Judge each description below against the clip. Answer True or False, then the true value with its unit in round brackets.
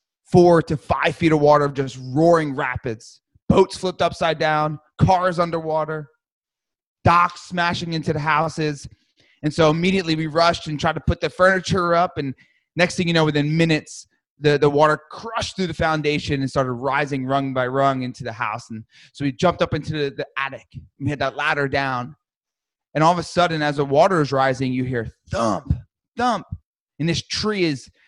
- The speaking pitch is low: False (155 Hz)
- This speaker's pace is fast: False (190 wpm)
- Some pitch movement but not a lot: True (3.5 semitones)